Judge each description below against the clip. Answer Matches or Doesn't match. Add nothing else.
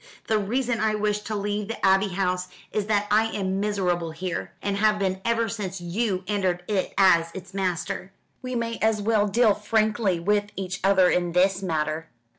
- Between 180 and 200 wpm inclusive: Matches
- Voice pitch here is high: Matches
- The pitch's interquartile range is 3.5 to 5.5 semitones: Doesn't match